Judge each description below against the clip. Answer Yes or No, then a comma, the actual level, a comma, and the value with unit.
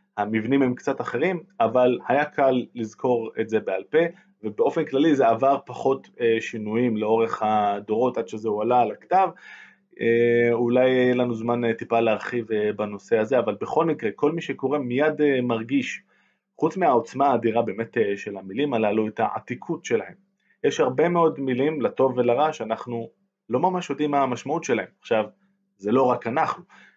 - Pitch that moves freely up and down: No, average, 4.4 semitones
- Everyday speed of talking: No, fast, 155 wpm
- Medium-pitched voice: No, low, 125 Hz